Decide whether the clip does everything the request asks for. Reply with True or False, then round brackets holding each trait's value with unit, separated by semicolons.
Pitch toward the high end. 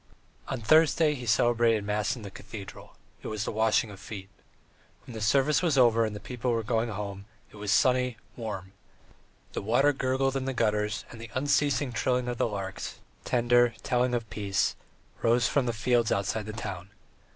False (115 Hz)